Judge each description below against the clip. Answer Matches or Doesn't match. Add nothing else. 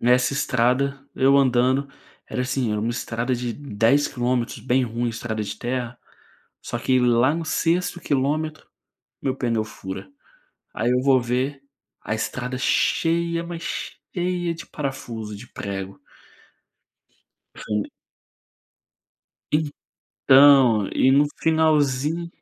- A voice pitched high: Doesn't match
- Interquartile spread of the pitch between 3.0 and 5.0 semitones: Matches